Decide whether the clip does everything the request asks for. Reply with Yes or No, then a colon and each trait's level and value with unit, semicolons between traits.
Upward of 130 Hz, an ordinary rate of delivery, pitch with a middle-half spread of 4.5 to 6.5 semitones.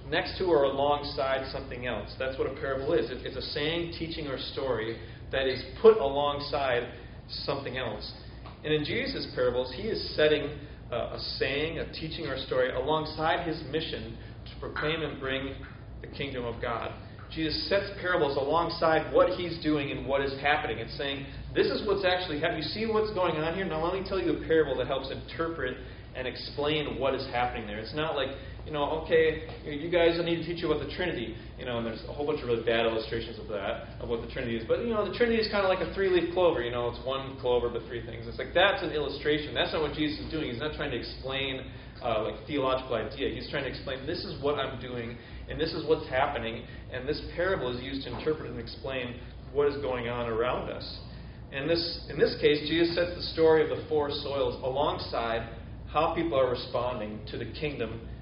No: medium, 140 Hz; fast, 220 wpm; average, 4.9 semitones